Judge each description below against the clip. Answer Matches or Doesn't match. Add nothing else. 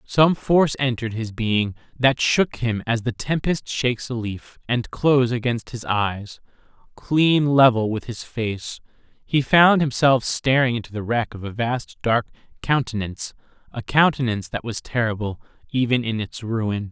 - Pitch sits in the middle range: Doesn't match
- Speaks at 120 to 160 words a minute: Matches